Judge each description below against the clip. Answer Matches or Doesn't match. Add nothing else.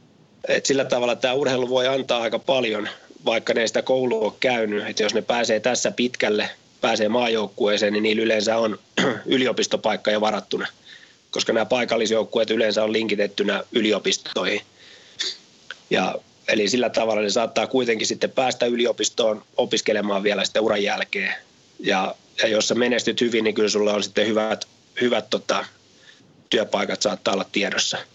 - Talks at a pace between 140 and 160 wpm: Matches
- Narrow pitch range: Matches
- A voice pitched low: Matches